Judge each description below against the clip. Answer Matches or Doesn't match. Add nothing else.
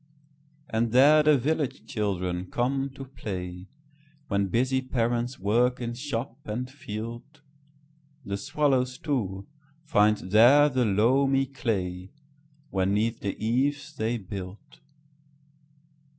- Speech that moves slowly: Matches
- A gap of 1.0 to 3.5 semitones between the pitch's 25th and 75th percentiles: Doesn't match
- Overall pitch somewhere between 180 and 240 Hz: Doesn't match